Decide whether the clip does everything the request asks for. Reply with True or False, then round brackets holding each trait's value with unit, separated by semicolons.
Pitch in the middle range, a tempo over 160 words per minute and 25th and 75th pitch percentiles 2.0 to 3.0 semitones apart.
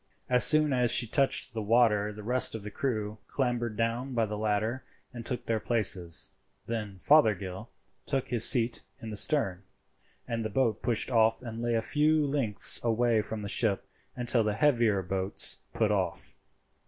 False (115 Hz; 175 wpm; 2.7 semitones)